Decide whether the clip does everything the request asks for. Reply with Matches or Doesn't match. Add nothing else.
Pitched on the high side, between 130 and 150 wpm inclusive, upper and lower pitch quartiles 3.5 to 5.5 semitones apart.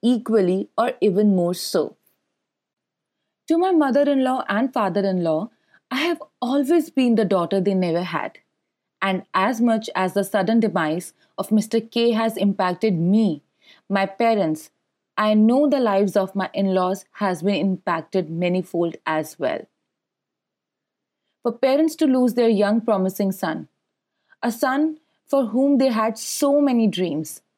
Matches